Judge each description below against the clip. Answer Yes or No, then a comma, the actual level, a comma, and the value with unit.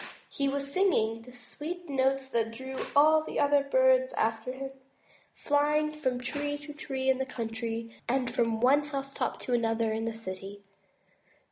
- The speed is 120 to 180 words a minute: Yes, average, 165 wpm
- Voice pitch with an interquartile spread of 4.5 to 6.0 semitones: No, average, 4.1 semitones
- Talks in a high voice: Yes, very high, 265 Hz